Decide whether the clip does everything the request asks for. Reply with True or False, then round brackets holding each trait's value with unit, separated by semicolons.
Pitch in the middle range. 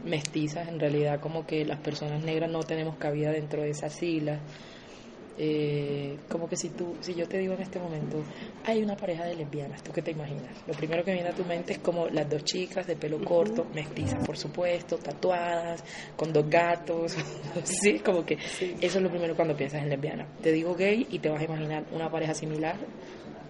True (165 Hz)